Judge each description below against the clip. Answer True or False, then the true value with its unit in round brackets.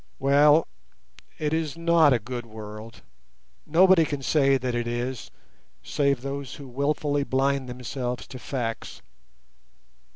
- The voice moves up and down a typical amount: True (3.2 semitones)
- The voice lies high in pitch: False (135 Hz)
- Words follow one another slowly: True (120 wpm)